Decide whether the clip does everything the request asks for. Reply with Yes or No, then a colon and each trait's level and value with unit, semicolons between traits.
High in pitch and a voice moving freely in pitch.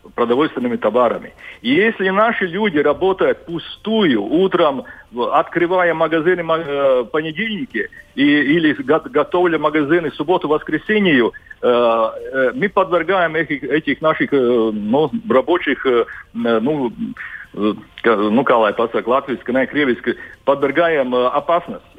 No: medium, 170 Hz; wide, 6.9 semitones